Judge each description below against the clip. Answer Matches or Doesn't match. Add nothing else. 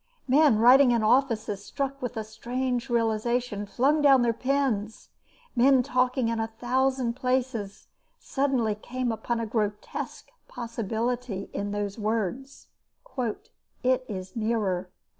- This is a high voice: Matches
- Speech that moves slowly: Matches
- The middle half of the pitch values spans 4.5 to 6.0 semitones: Doesn't match